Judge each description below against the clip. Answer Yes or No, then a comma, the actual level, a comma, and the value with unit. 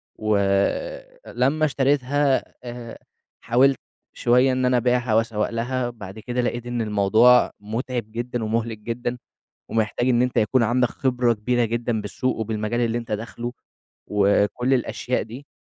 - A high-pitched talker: No, low, 120 Hz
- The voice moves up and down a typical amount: No, narrow, 2.1 semitones